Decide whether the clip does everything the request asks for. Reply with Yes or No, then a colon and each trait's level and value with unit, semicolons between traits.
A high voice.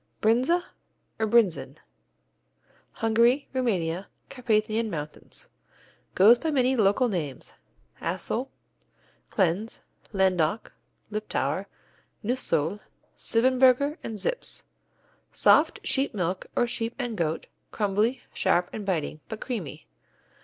Yes: high, 220 Hz